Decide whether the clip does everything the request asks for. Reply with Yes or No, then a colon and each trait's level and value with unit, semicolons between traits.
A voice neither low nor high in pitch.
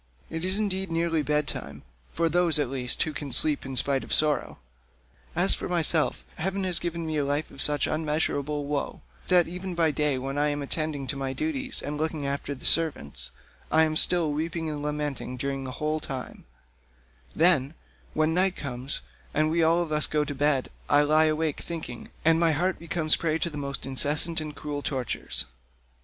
Yes: medium, 150 Hz